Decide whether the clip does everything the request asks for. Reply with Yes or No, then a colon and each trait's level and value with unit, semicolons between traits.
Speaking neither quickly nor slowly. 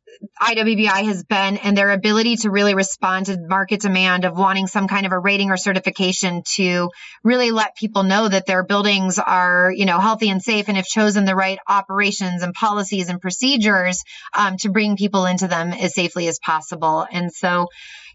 Yes: average, 190 wpm